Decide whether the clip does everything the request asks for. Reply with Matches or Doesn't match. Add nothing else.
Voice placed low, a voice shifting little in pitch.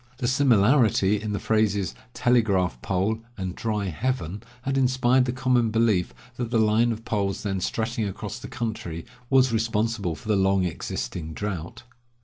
Doesn't match